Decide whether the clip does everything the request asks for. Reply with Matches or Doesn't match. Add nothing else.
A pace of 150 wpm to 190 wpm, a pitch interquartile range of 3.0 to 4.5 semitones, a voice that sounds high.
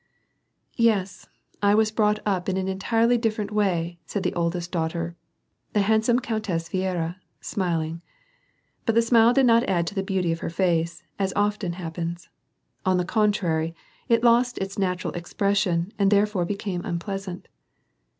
Matches